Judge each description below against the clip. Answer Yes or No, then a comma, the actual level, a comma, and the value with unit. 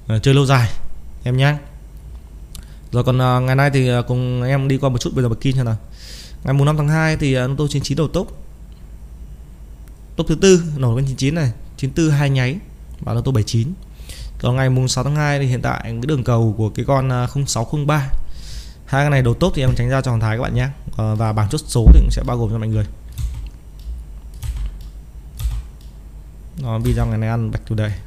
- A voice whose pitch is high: No, low, 120 Hz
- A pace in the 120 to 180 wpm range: No, average, 205 wpm